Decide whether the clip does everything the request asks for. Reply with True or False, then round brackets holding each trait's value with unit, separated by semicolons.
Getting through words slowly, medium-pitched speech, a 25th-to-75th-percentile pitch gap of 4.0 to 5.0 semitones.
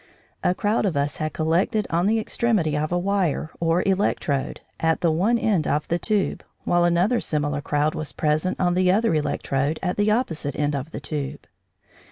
False (190 wpm; 170 Hz; 4.5 semitones)